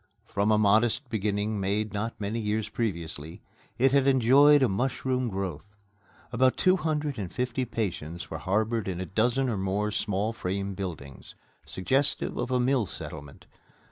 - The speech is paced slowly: No, average, 155 wpm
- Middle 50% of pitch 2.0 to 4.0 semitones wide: No, average, 4.5 semitones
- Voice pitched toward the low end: Yes, low, 110 Hz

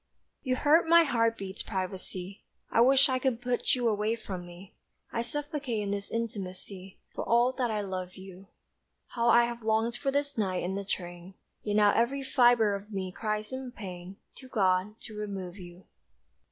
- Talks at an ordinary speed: Yes, average, 180 wpm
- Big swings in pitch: No, average, 4.2 semitones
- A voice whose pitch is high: Yes, high, 215 Hz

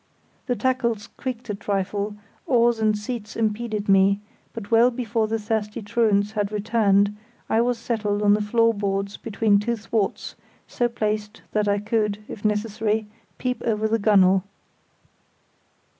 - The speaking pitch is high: Yes, high, 215 Hz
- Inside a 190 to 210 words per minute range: No, average, 145 wpm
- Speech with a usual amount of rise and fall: No, narrow, 2.0 semitones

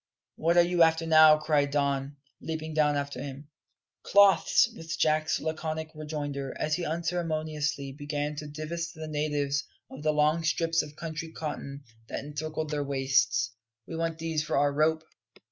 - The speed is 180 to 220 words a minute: No, average, 160 wpm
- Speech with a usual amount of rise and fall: No, narrow, 1.8 semitones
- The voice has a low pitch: No, medium, 155 Hz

